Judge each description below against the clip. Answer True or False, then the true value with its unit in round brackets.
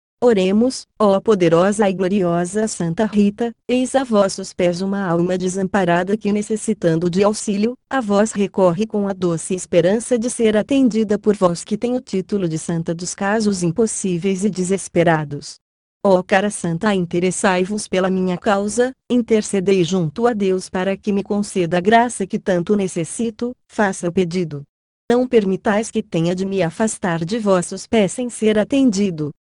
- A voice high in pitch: True (195 Hz)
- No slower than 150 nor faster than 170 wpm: True (155 wpm)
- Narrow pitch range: False (3.1 semitones)